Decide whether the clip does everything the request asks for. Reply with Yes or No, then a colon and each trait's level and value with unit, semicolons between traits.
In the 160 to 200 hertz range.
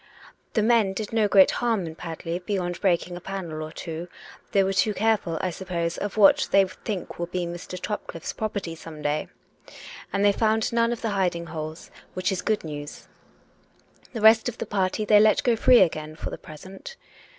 Yes: high, 190 Hz